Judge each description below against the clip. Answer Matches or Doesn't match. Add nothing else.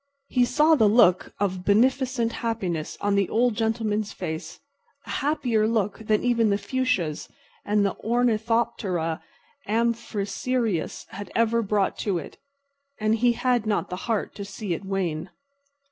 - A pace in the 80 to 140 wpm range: Matches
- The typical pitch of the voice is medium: Doesn't match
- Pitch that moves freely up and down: Doesn't match